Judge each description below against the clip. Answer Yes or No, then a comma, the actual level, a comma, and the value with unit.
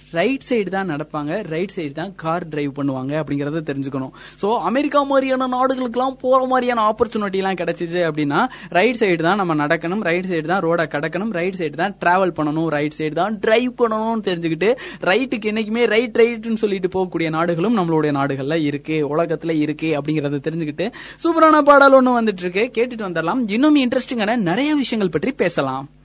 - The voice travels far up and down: Yes, wide, 6.7 semitones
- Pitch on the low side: No, medium, 185 Hz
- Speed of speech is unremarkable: No, fast, 165 wpm